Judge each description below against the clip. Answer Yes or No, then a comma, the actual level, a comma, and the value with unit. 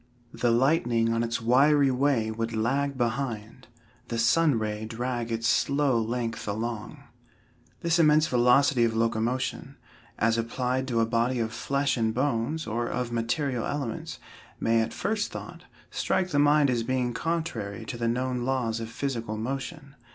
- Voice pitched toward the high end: No, low, 120 Hz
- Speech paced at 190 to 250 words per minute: No, average, 155 wpm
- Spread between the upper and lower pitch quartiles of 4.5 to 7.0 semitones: No, average, 3.2 semitones